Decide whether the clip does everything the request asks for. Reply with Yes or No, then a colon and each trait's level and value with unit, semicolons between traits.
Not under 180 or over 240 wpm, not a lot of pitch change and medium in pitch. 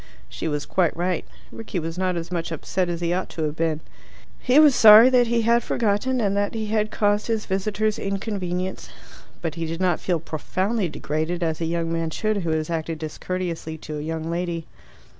No: average, 200 wpm; average, 4.2 semitones; medium, 180 Hz